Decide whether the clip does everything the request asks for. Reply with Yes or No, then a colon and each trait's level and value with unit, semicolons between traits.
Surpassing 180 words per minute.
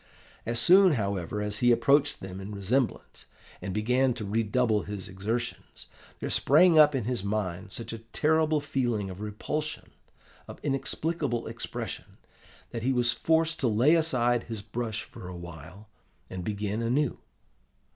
No: average, 150 wpm